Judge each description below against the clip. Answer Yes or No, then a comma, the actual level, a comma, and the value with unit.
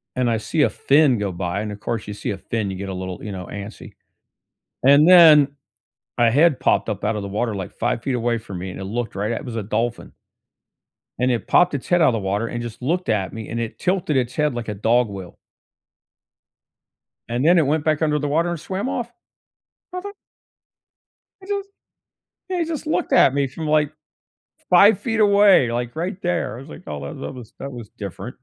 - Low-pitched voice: Yes, low, 125 Hz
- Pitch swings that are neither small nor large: No, wide, 6.9 semitones